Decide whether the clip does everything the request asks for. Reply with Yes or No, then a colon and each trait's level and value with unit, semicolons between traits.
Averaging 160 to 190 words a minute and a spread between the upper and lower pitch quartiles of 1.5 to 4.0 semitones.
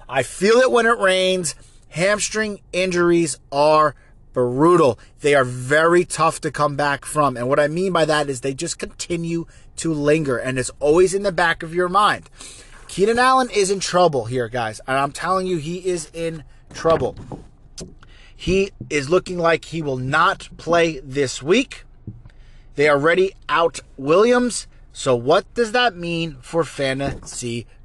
No: average, 165 wpm; average, 5.1 semitones